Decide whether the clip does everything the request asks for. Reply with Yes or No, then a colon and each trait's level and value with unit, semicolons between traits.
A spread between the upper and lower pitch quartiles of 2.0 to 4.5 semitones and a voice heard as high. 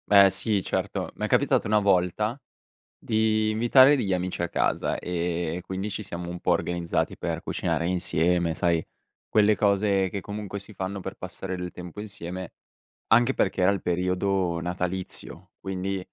No: average, 2.7 semitones; very low, 95 Hz